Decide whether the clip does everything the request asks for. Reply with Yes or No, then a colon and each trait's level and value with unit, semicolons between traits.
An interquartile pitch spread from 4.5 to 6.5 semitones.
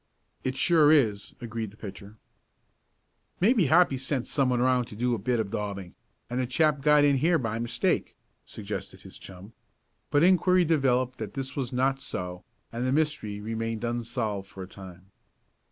Yes: average, 4.8 semitones